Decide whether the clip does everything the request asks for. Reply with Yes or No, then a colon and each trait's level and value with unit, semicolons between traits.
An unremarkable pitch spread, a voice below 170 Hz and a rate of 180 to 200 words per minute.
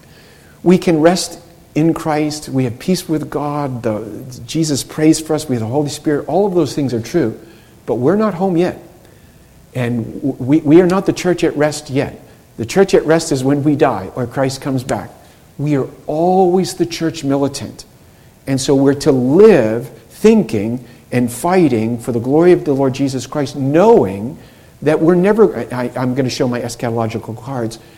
Yes: average, 4.8 semitones; medium, 140 Hz; average, 190 wpm